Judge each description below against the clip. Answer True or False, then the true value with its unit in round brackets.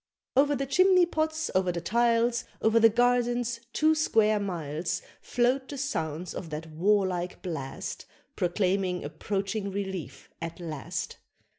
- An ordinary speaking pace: False (130 wpm)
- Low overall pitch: False (205 Hz)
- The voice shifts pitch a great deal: True (5.7 semitones)